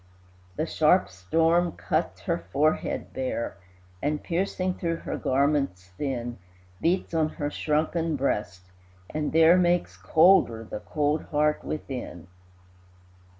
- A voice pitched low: No, medium, 150 Hz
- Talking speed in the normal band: No, slow, 115 wpm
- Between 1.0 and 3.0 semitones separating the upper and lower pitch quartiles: No, average, 4.8 semitones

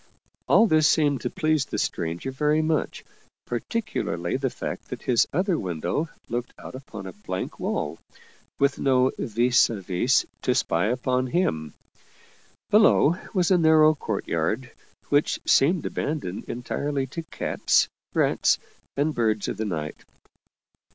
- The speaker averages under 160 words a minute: Yes, average, 140 wpm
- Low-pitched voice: Yes, low, 130 Hz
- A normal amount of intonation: No, wide, 6.5 semitones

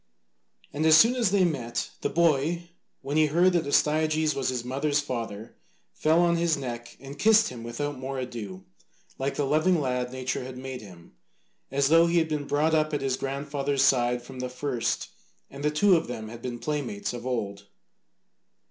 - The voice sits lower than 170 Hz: Yes, medium, 140 Hz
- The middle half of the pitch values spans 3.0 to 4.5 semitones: Yes, average, 4.0 semitones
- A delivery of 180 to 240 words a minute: Yes, average, 190 wpm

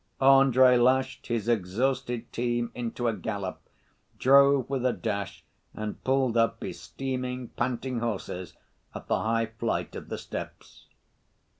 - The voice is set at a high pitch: No, low, 120 Hz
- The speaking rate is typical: No, slow, 130 wpm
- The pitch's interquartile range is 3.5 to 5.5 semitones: No, narrow, 2.4 semitones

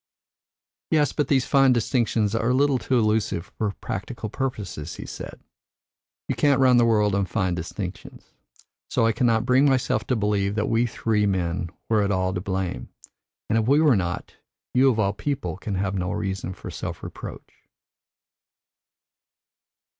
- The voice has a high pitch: No, low, 110 Hz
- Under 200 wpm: Yes, average, 165 wpm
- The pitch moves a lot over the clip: No, average, 4.5 semitones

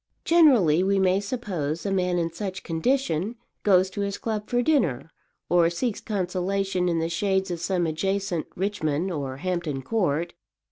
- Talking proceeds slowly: No, average, 160 wpm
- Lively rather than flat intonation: No, average, 3.2 semitones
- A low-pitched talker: No, medium, 185 Hz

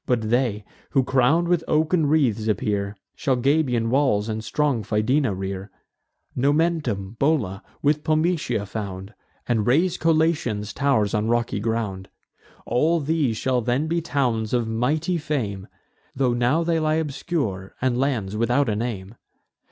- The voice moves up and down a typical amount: No, wide, 5.9 semitones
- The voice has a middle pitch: No, low, 125 Hz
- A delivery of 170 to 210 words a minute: No, average, 140 wpm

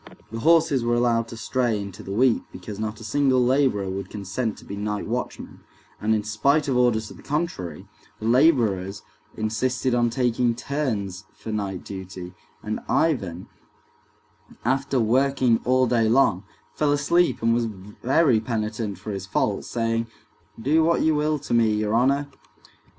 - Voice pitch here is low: Yes, low, 115 Hz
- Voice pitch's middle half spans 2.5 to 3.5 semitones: No, average, 3.9 semitones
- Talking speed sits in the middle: Yes, average, 160 wpm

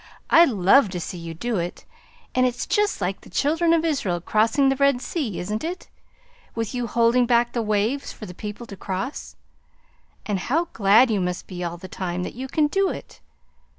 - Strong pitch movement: Yes, wide, 6.4 semitones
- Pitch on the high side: Yes, high, 230 Hz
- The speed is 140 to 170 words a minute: No, average, 200 wpm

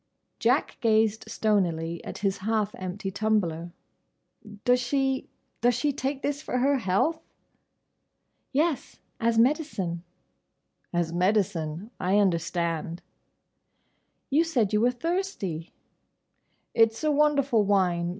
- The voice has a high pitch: Yes, high, 215 Hz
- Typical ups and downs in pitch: No, wide, 6.7 semitones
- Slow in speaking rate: Yes, slow, 100 wpm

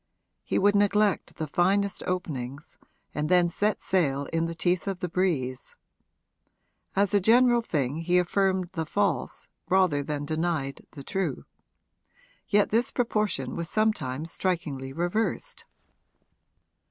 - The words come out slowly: Yes, slow, 130 wpm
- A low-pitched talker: No, medium, 175 Hz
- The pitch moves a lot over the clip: No, average, 5.0 semitones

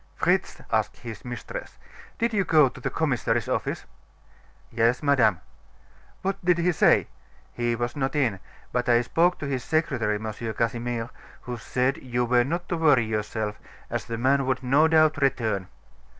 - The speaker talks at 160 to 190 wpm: Yes, average, 165 wpm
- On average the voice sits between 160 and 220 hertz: No, low, 125 Hz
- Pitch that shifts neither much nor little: Yes, average, 4.6 semitones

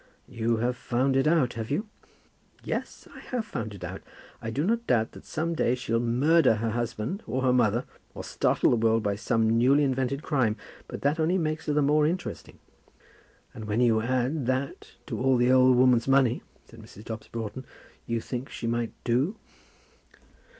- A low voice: Yes, low, 125 Hz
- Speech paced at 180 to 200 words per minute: Yes, average, 190 wpm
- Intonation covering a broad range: No, average, 3.7 semitones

